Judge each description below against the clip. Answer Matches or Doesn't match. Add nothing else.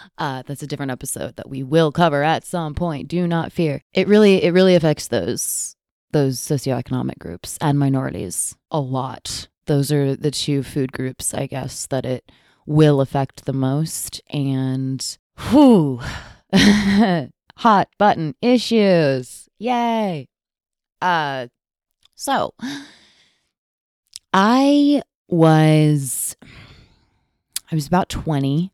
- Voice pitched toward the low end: Doesn't match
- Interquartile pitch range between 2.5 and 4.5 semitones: Doesn't match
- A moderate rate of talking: Doesn't match